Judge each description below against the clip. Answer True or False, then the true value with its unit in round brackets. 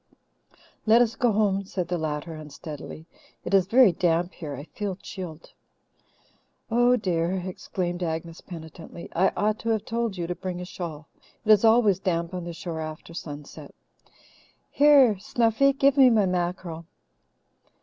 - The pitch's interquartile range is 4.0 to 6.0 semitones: True (4.5 semitones)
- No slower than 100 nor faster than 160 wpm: True (155 wpm)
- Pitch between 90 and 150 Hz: False (180 Hz)